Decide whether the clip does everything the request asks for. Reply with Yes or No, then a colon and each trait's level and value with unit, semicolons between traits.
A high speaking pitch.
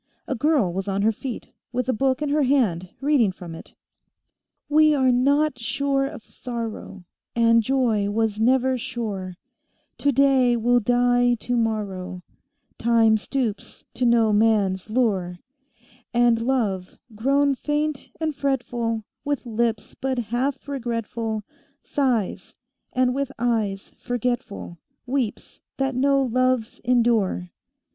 Yes: high, 240 Hz